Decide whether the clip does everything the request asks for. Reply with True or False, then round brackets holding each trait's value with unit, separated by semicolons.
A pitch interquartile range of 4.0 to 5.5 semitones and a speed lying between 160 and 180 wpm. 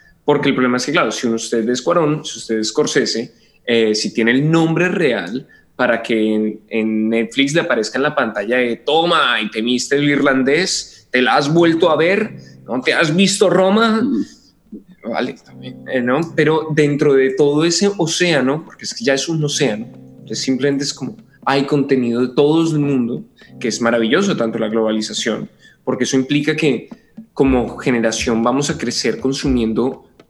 True (5.2 semitones; 175 wpm)